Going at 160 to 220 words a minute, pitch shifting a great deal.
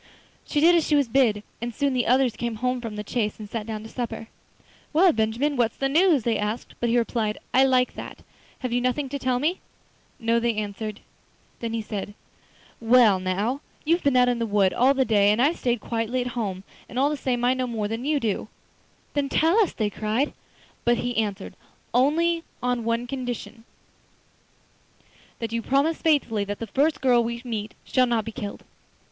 No: average, 200 wpm; average, 3.4 semitones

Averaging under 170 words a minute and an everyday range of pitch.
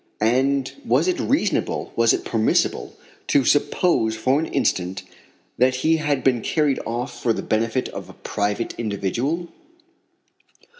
Yes: average, 140 wpm; average, 4.6 semitones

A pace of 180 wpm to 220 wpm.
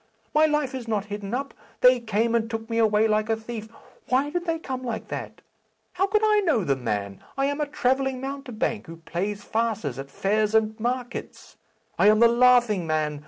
Yes: average, 200 wpm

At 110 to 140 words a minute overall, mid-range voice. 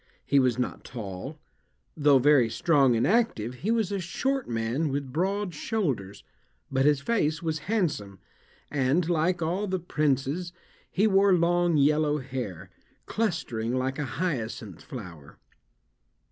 Yes: slow, 135 wpm; medium, 150 Hz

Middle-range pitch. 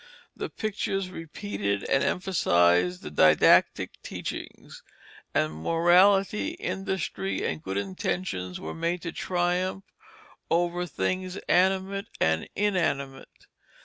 Yes: medium, 175 Hz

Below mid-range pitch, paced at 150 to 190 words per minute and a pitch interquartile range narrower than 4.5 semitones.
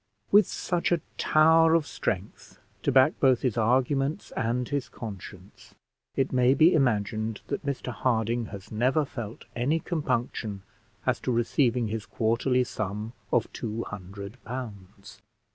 No: low, 120 Hz; average, 140 wpm; average, 4.1 semitones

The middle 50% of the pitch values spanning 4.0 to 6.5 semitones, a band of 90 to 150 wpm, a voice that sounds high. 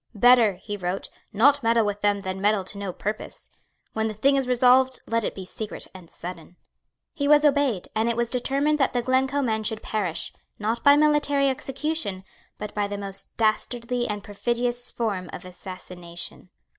No: average, 4.5 semitones; average, 180 wpm; high, 220 Hz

